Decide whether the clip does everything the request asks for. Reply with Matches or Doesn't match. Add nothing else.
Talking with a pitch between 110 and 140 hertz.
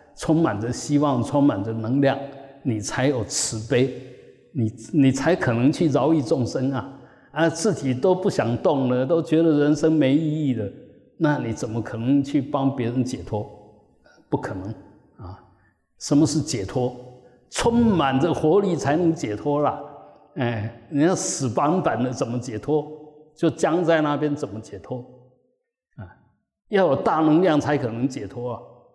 Matches